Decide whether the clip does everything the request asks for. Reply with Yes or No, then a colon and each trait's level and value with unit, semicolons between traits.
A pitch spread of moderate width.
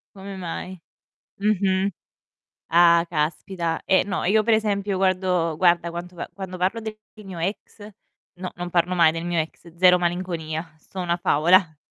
No: narrow, 2.1 semitones